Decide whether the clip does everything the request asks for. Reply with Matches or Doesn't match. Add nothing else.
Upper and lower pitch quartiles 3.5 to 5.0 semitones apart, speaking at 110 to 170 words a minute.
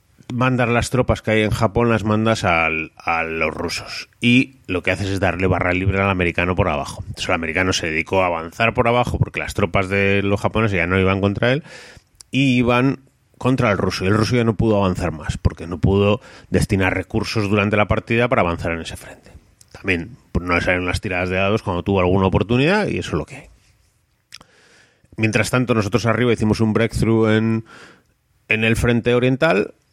Doesn't match